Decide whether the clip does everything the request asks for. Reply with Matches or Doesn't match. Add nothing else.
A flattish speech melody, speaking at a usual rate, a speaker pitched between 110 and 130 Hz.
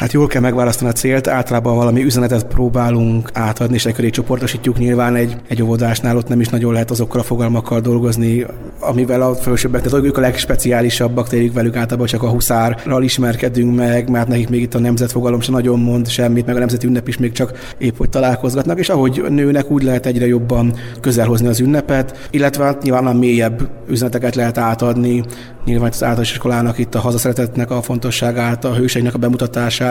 Doesn't match